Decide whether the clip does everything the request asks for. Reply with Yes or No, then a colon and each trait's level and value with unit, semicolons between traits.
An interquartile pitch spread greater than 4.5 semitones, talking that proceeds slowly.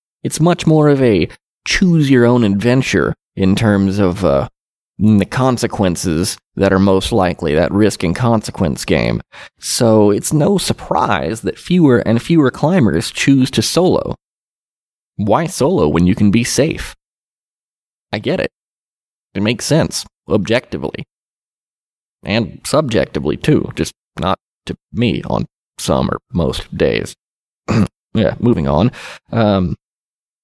Yes: average, 5.1 semitones; slow, 130 wpm